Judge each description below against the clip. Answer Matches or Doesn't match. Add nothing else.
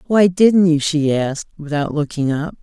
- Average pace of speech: Matches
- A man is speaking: Doesn't match